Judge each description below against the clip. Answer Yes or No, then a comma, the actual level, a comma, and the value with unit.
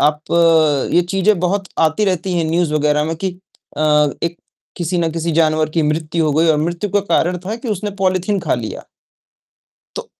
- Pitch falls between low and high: Yes, medium, 170 Hz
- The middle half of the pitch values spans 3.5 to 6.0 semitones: No, average, 3.1 semitones